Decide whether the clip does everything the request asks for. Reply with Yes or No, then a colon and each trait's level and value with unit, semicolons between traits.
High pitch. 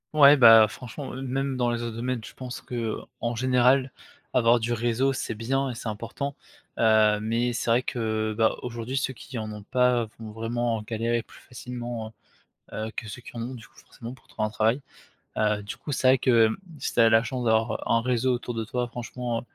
No: low, 120 Hz